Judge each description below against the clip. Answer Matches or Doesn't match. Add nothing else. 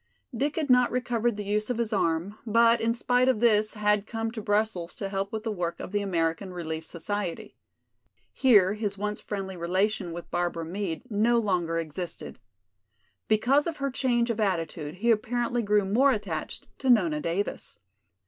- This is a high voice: Matches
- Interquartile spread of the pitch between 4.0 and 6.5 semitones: Matches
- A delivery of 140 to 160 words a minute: Doesn't match